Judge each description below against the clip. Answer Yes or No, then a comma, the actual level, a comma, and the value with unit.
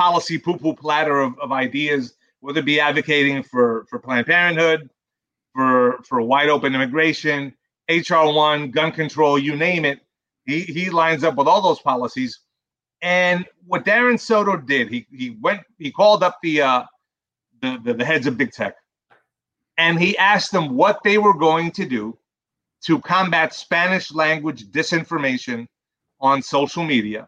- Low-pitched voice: No, medium, 160 Hz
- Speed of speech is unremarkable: Yes, average, 155 wpm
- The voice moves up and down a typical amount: Yes, average, 3.9 semitones